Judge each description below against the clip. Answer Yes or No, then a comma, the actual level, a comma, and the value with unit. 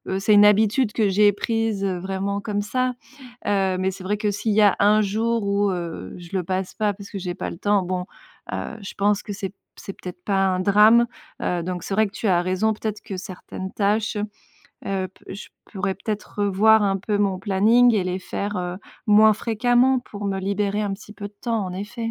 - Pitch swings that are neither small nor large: No, narrow, 2.1 semitones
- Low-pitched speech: No, high, 200 Hz